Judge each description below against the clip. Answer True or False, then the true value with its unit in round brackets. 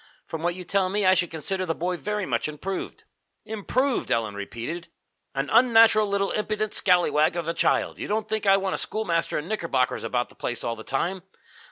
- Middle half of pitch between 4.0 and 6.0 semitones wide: True (5.0 semitones)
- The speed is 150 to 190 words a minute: False (200 wpm)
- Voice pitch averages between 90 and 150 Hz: False (185 Hz)